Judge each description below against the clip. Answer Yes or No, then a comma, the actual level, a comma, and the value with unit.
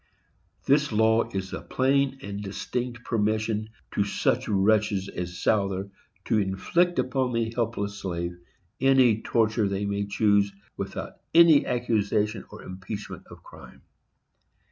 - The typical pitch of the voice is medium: No, low, 110 Hz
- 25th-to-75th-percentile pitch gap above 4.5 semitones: No, average, 3.2 semitones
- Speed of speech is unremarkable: No, slow, 125 wpm